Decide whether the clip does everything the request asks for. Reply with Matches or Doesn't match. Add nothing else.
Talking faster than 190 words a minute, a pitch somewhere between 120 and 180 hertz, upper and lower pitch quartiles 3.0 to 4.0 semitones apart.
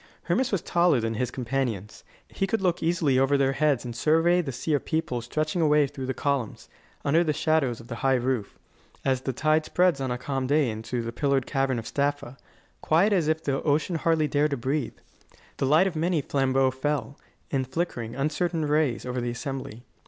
Matches